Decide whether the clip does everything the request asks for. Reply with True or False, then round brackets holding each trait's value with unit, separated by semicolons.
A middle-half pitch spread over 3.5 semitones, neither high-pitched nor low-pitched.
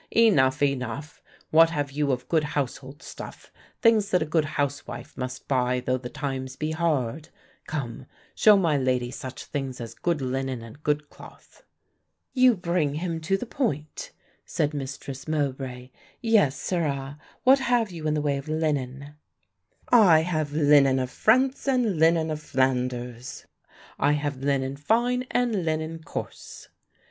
True (3.9 semitones; 145 Hz)